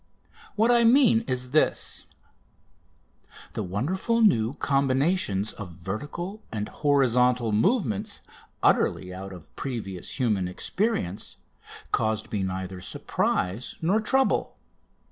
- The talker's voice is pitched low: Yes, low, 125 Hz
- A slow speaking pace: Yes, slow, 105 wpm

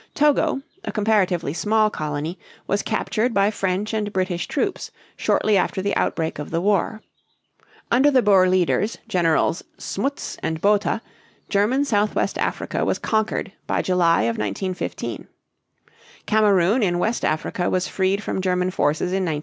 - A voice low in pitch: No, high, 195 Hz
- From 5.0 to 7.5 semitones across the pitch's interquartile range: No, average, 3.4 semitones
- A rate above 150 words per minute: No, average, 145 wpm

